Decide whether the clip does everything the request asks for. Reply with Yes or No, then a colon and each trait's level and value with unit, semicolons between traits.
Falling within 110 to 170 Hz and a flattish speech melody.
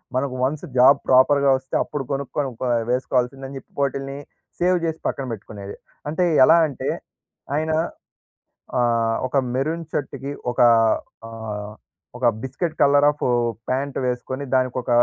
Yes: low, 135 Hz; narrow, 2.3 semitones